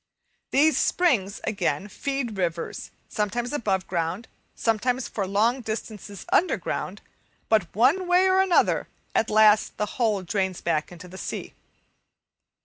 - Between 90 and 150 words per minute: Yes, slow, 135 wpm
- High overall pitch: Yes, high, 215 Hz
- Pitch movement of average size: Yes, average, 4.9 semitones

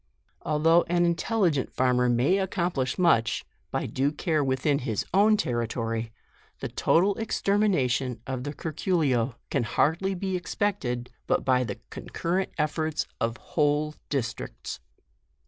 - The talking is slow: Yes, slow, 130 wpm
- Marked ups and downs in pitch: Yes, wide, 5.9 semitones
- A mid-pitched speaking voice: Yes, medium, 150 Hz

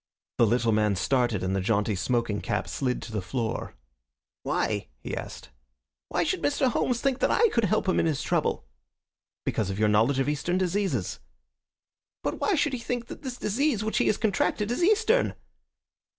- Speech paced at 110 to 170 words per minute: No, average, 185 wpm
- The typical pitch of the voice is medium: Yes, medium, 165 Hz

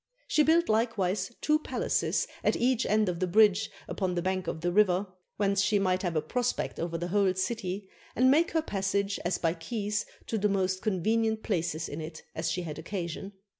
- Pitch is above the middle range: Yes, high, 195 Hz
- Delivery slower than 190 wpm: No, fast, 205 wpm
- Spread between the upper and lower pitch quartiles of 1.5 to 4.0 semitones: Yes, average, 3.7 semitones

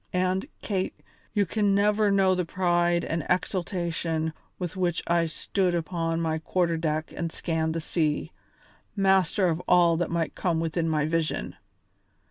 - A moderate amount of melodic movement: No, narrow, 2.3 semitones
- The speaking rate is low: No, average, 150 wpm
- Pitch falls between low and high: Yes, medium, 170 Hz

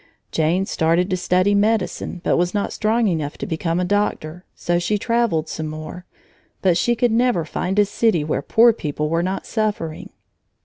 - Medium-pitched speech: Yes, medium, 180 Hz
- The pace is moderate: Yes, average, 180 wpm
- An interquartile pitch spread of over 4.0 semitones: Yes, average, 4.6 semitones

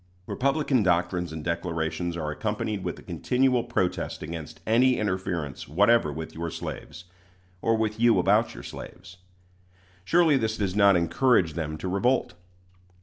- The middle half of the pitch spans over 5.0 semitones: Yes, wide, 5.5 semitones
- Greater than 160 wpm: No, average, 145 wpm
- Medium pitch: No, very low, 95 Hz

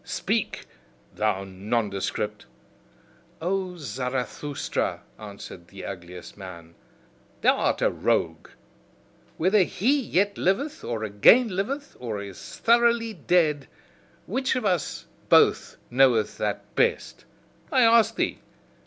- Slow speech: Yes, slow, 110 wpm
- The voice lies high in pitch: No, medium, 150 Hz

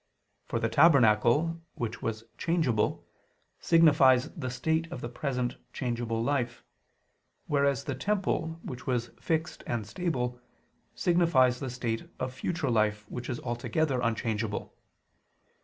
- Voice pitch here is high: No, low, 125 Hz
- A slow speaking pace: Yes, slow, 125 wpm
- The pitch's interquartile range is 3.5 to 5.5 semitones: Yes, average, 5.0 semitones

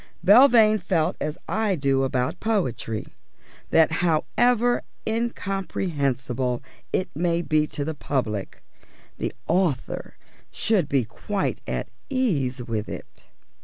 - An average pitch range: No, wide, 7.3 semitones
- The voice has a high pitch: No, medium, 160 Hz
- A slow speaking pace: Yes, slow, 110 wpm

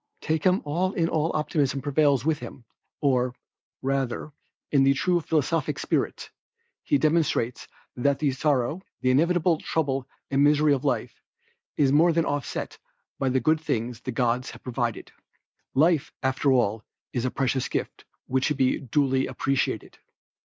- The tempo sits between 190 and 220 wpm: No, average, 150 wpm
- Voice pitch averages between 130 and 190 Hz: Yes, medium, 140 Hz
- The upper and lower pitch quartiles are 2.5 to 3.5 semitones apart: Yes, average, 3.2 semitones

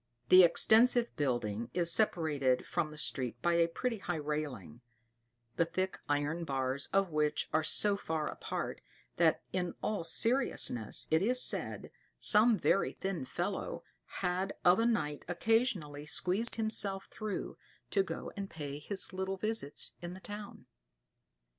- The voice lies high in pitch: No, medium, 175 Hz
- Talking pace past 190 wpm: No, average, 145 wpm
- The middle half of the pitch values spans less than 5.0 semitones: No, wide, 5.5 semitones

